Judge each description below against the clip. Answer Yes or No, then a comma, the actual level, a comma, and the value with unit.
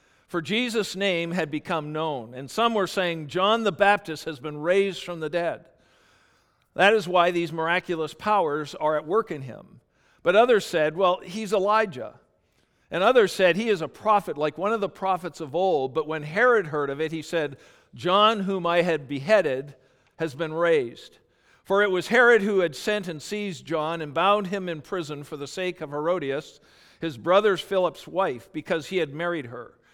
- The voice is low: No, medium, 175 Hz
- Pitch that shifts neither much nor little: Yes, average, 4.1 semitones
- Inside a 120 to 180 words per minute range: No, average, 190 wpm